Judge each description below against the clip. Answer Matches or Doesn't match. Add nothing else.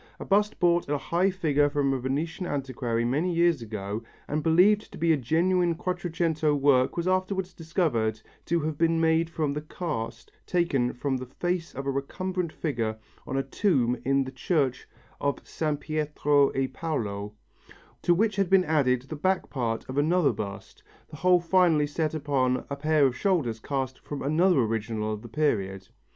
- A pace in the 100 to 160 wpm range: Doesn't match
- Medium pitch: Matches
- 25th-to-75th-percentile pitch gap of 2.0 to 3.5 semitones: Doesn't match